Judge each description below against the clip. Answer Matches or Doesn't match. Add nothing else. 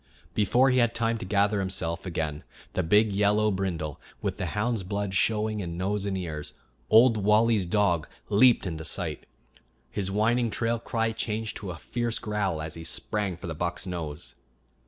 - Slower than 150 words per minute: Doesn't match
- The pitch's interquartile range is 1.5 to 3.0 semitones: Doesn't match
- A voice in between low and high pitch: Doesn't match